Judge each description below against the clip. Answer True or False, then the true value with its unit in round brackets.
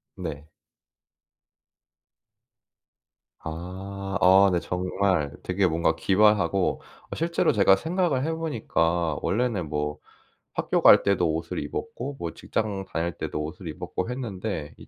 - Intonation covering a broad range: False (4.6 semitones)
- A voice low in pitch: True (95 Hz)